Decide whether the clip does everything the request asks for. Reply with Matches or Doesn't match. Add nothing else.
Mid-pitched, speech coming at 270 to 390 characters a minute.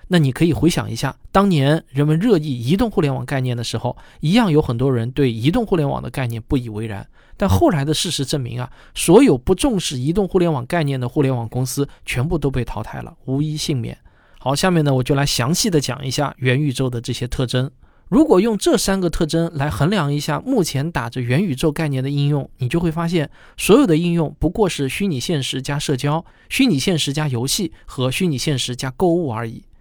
Matches